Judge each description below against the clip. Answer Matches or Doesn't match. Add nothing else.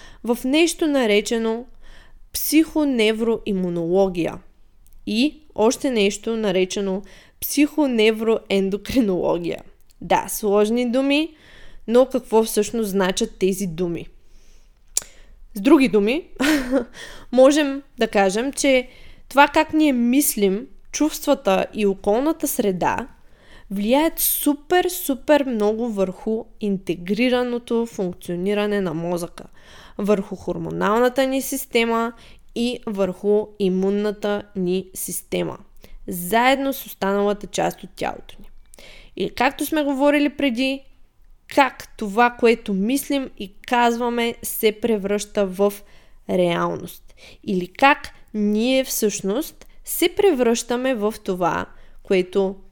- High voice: Matches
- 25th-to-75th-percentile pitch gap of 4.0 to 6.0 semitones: Matches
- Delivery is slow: Matches